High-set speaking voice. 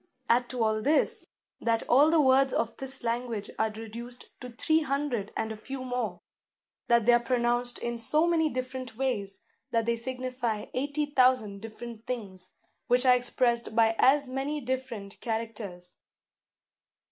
Yes: high, 245 Hz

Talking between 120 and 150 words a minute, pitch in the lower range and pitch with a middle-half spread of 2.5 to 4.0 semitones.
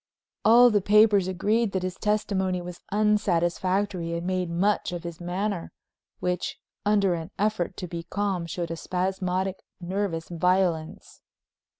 No: slow, 135 wpm; medium, 185 Hz; average, 2.8 semitones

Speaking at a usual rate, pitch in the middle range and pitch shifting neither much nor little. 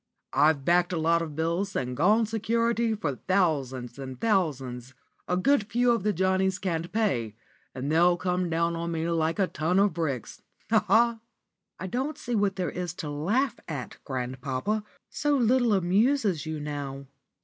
No: average, 170 wpm; medium, 175 Hz; wide, 6.1 semitones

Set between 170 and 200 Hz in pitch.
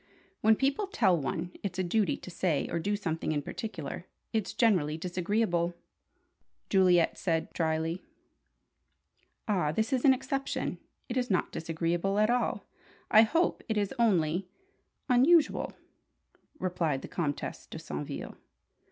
Yes: medium, 185 Hz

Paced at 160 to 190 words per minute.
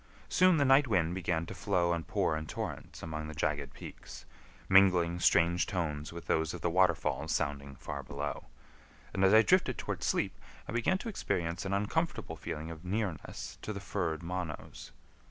Yes: average, 175 wpm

